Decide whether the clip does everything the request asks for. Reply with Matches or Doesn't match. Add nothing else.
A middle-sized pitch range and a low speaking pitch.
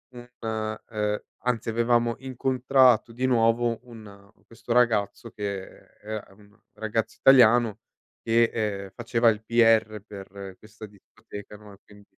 Doesn't match